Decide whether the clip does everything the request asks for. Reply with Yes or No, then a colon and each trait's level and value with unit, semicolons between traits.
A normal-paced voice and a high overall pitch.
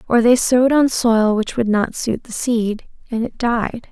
No: fast, 215 wpm; high, 230 Hz